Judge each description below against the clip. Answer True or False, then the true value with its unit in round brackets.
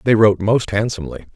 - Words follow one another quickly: False (180 wpm)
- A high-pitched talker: False (105 Hz)